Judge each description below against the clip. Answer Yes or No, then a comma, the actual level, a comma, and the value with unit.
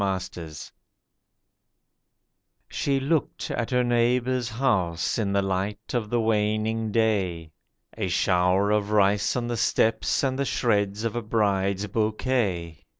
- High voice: No, low, 105 Hz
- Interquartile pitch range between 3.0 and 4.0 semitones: Yes, average, 3.4 semitones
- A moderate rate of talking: No, slow, 130 wpm